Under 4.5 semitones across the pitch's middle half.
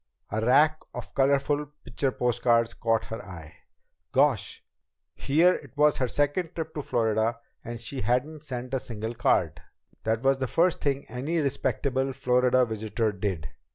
Yes: average, 4.0 semitones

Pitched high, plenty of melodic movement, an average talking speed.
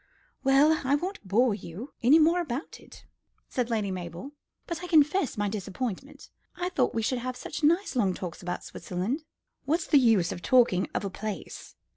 Yes: very high, 250 Hz; wide, 7.1 semitones; average, 180 wpm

